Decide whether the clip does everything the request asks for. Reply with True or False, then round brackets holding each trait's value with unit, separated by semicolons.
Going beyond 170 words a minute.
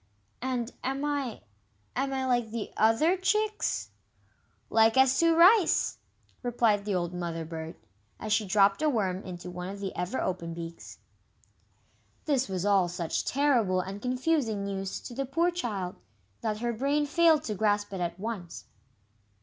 False (160 wpm)